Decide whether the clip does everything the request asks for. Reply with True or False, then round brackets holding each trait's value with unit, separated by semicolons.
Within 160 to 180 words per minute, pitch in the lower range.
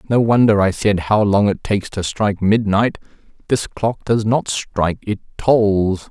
True (175 wpm; 105 Hz)